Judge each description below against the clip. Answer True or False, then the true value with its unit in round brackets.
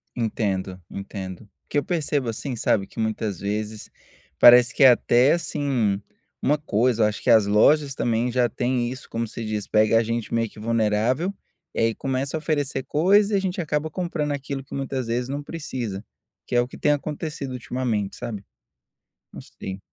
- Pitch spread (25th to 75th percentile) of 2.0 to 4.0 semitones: False (4.9 semitones)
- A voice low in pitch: True (120 Hz)